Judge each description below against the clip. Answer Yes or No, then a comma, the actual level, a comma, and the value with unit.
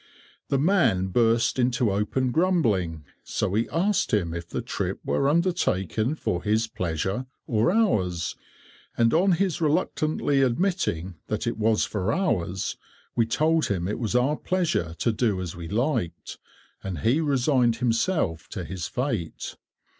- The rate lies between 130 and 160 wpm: Yes, average, 145 wpm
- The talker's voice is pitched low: Yes, low, 115 Hz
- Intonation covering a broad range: Yes, wide, 8.1 semitones